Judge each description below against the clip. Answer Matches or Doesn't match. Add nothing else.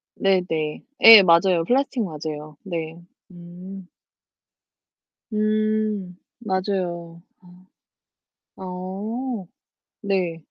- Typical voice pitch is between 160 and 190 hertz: Matches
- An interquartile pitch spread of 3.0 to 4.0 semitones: Matches